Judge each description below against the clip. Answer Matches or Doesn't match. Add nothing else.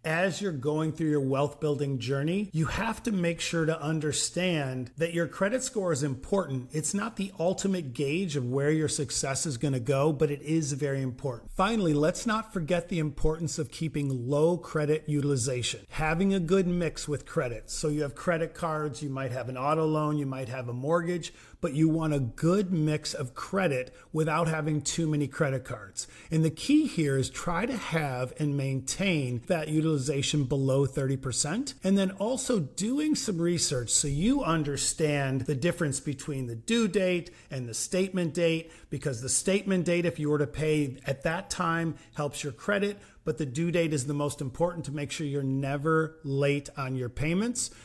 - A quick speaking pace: Doesn't match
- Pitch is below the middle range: Doesn't match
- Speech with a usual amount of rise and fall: Matches